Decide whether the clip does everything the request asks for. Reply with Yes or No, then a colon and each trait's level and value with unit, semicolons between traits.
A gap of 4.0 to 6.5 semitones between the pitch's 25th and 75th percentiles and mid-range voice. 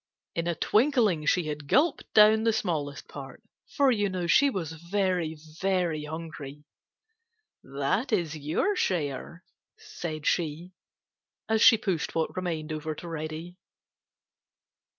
Yes: average, 4.9 semitones; medium, 170 Hz